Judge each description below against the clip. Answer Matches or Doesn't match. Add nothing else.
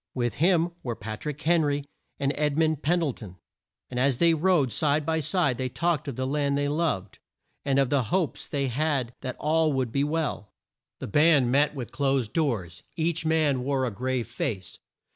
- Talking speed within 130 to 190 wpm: Doesn't match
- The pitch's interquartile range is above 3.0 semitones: Matches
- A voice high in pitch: Doesn't match